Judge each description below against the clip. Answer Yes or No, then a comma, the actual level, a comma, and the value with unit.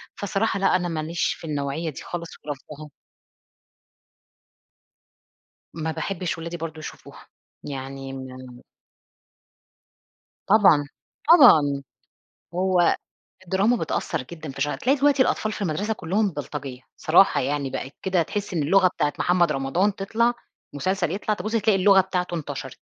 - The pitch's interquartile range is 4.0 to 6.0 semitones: Yes, average, 5.1 semitones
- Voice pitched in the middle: Yes, medium, 170 Hz